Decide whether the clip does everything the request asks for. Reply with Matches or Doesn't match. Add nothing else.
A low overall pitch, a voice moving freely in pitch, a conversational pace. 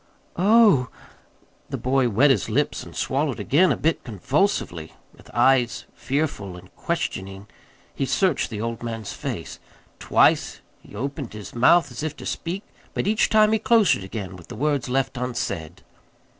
Matches